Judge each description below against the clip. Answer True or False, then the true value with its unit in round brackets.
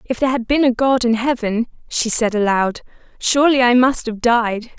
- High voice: True (240 Hz)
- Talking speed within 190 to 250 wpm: True (200 wpm)